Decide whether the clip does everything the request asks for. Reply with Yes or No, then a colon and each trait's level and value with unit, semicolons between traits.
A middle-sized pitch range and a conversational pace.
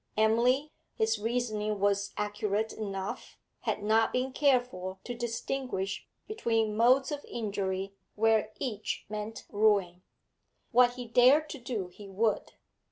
No: average, 3.2 semitones; slow, 125 wpm